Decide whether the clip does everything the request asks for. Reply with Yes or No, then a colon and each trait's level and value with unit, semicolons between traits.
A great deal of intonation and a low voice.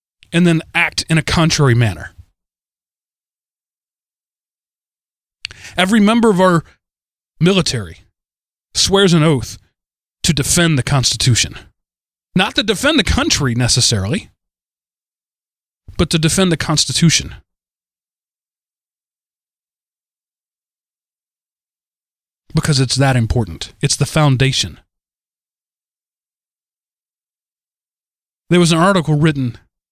No: wide, 6.4 semitones; medium, 145 Hz